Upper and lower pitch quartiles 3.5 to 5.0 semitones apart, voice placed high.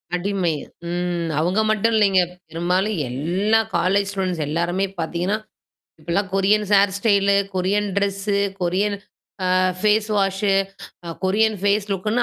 No: narrow, 2.5 semitones; high, 195 Hz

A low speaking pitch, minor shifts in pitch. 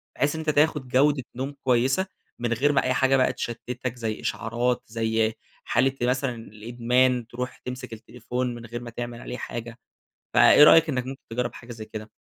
Yes: low, 125 Hz; narrow, 2.0 semitones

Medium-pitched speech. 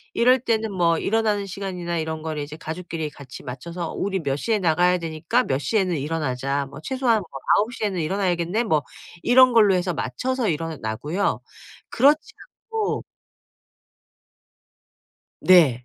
Yes: medium, 175 Hz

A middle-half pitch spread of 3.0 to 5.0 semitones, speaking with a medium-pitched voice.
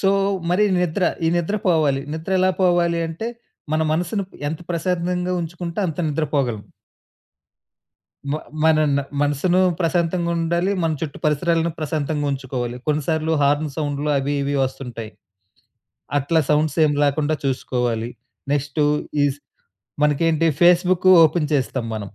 Yes: average, 3.3 semitones; medium, 155 Hz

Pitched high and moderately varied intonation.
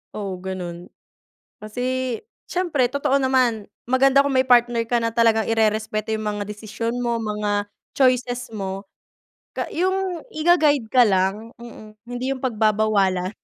Yes: high, 230 Hz; average, 3.6 semitones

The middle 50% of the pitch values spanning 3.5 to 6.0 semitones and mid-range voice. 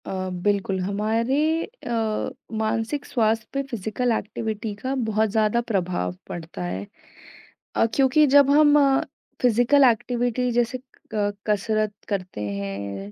No: average, 3.9 semitones; high, 220 Hz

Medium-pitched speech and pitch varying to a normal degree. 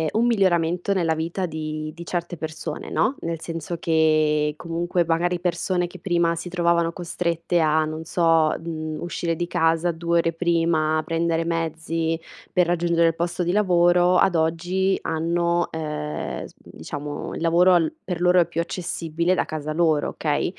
No: medium, 170 Hz; narrow, 1.5 semitones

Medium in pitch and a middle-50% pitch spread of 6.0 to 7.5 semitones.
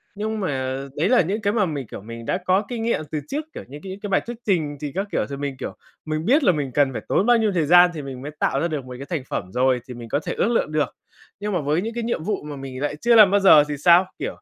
Yes: medium, 160 Hz; wide, 6.5 semitones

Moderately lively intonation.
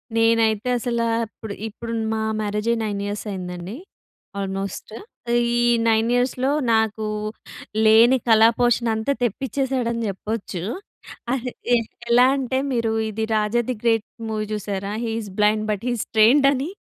No: narrow, 2.3 semitones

